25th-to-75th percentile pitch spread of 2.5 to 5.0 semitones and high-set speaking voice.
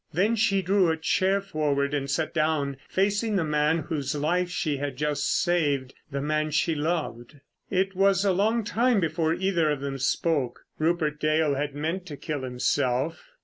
No: average, 4.3 semitones; medium, 155 Hz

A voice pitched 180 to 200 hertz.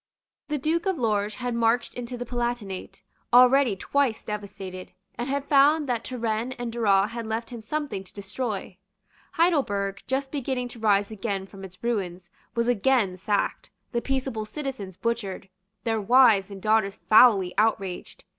No: high, 230 Hz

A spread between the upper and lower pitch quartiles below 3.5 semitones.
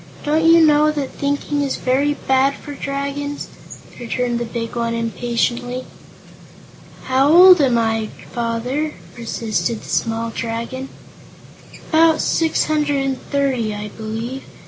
No: average, 3.9 semitones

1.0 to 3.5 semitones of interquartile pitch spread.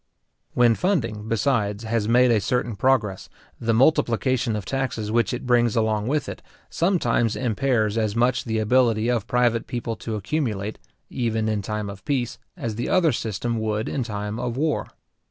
Yes: narrow, 2.6 semitones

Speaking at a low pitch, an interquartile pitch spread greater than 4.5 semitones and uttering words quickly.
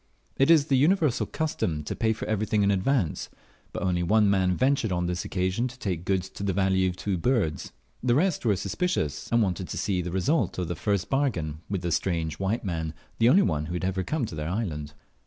Yes: very low, 95 Hz; average, 5.2 semitones; fast, 225 wpm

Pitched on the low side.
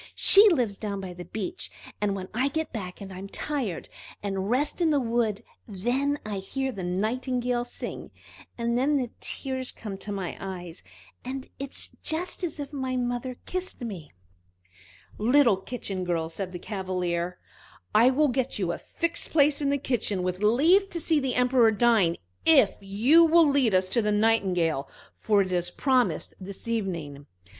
No: high, 230 Hz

